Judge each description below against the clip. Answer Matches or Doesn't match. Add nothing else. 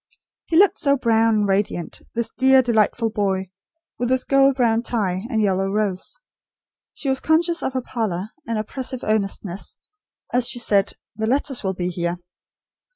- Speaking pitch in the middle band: Doesn't match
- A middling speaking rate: Matches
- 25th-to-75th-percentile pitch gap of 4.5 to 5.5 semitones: Matches